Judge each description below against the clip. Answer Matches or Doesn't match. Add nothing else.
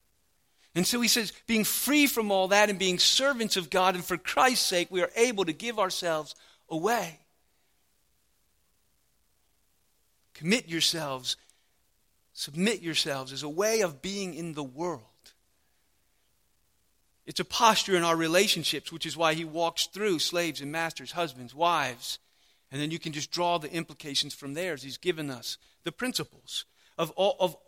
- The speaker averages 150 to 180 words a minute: Matches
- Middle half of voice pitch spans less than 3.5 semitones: Doesn't match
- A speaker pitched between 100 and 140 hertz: Doesn't match